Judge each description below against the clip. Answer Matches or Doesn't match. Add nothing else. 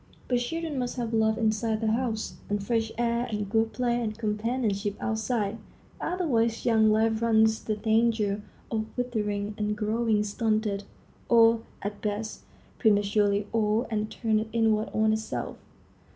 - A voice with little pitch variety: Matches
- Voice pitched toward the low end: Doesn't match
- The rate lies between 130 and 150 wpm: Matches